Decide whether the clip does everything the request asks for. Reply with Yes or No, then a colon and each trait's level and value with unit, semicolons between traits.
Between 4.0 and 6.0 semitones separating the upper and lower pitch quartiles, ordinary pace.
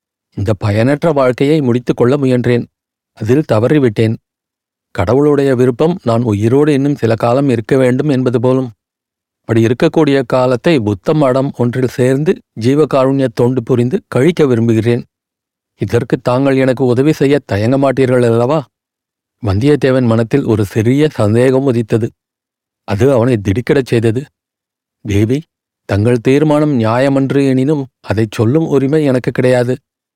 No: average, 3.2 semitones; average, 115 wpm